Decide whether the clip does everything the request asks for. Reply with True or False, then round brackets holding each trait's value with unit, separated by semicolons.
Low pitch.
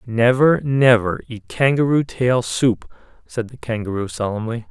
True (120 Hz)